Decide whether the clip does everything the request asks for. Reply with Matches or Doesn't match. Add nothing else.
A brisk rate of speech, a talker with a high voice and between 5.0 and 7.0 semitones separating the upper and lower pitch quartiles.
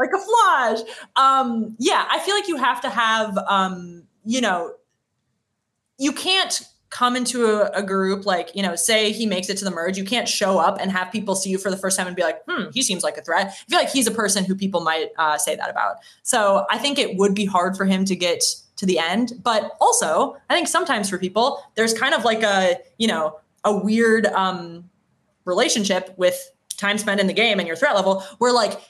Matches